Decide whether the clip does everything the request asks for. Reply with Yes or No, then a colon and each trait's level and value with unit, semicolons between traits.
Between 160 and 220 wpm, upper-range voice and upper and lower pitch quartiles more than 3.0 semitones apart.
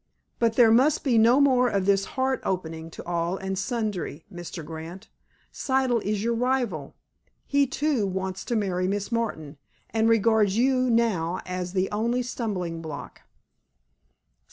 No: average, 150 wpm; high, 210 Hz; average, 4.8 semitones